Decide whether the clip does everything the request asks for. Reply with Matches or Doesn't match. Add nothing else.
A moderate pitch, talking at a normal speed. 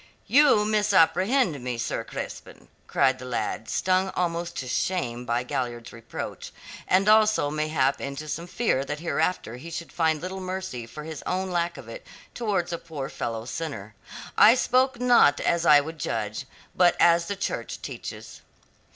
Matches